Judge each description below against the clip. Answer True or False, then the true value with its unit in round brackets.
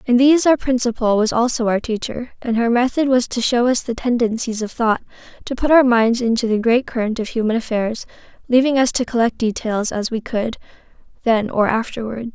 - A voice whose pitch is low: False (235 Hz)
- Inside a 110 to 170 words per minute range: False (200 wpm)